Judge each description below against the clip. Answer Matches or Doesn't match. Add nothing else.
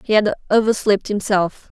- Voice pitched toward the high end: Matches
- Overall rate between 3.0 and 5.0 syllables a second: Matches